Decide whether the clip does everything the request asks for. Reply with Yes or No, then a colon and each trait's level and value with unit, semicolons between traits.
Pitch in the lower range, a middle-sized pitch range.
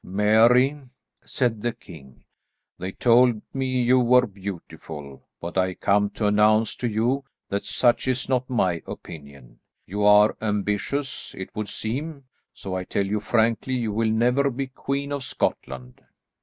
Yes: low, 110 Hz; average, 4.2 semitones